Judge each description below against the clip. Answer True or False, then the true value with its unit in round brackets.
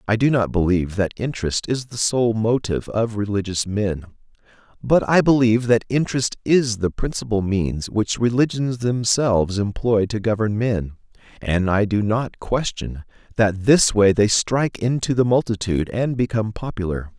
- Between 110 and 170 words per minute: True (155 wpm)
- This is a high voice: False (110 Hz)